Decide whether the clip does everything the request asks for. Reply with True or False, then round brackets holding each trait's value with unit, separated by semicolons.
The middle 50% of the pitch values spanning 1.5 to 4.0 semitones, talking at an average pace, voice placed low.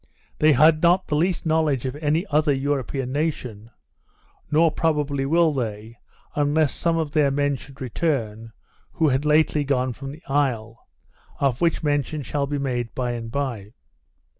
False (3.2 semitones; 160 wpm; 145 Hz)